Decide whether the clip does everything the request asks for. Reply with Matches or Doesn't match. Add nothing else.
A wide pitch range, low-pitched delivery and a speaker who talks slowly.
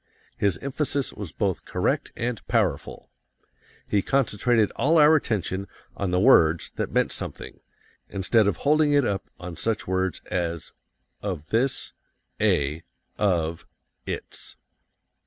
Matches